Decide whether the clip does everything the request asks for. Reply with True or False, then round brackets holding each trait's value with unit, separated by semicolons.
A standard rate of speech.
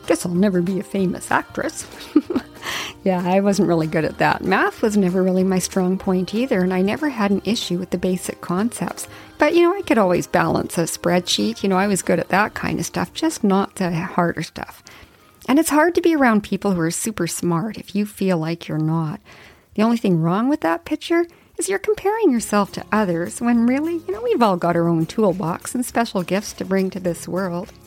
False (225 wpm)